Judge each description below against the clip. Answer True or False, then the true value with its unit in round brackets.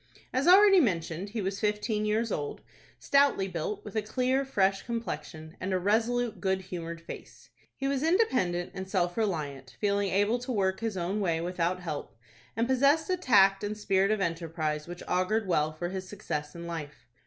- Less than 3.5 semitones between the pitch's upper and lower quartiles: False (4.7 semitones)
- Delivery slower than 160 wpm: False (180 wpm)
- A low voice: False (195 Hz)